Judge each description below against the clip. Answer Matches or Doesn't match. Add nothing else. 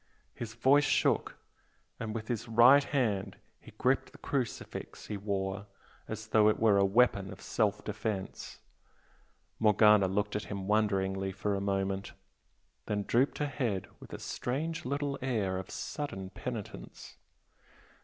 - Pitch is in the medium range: Doesn't match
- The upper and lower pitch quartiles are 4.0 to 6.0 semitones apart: Doesn't match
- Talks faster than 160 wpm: Doesn't match